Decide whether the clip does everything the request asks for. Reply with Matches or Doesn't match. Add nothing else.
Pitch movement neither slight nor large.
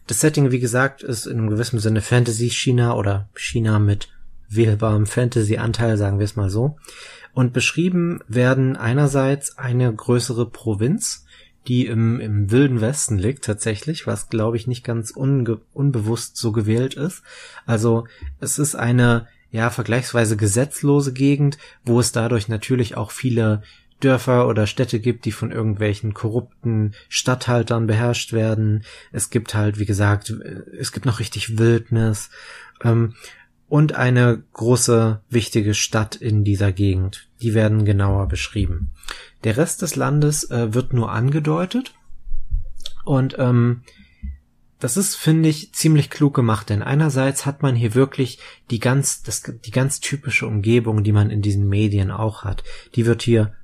Matches